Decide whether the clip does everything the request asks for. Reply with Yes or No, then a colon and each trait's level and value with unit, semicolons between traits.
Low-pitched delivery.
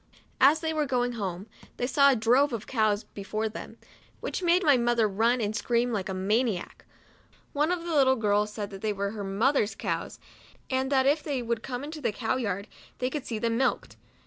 No: high, 235 Hz